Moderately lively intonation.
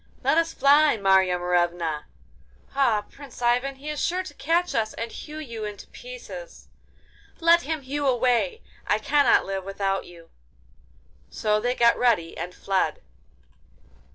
No: wide, 7.4 semitones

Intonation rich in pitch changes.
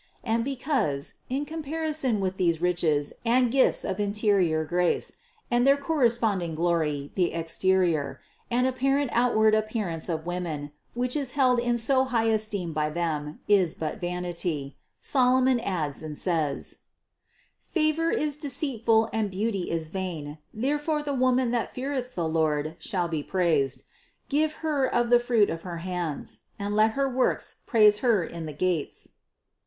Yes: wide, 7.2 semitones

